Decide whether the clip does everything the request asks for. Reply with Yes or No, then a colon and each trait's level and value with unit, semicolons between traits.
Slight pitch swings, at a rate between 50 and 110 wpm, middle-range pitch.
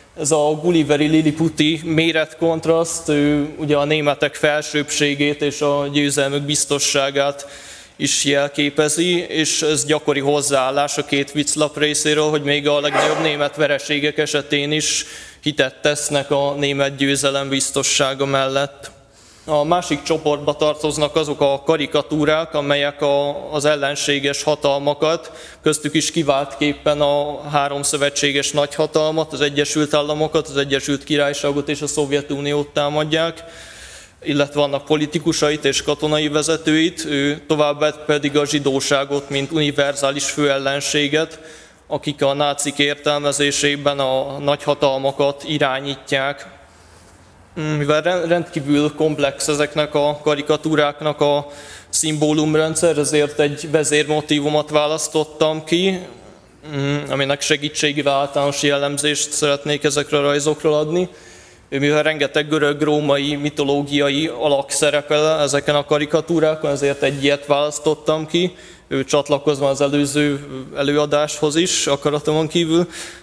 Yes: narrow, 1.2 semitones; slow, 105 wpm; medium, 150 Hz